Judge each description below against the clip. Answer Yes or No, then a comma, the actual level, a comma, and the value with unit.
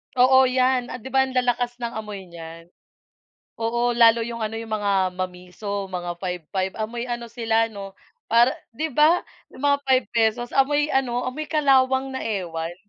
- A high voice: Yes, high, 235 Hz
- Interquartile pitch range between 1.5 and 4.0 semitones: No, average, 4.6 semitones